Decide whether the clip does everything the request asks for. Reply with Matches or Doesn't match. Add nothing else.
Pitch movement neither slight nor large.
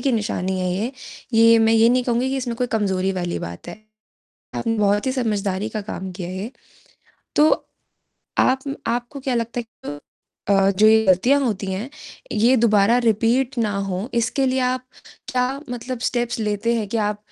Matches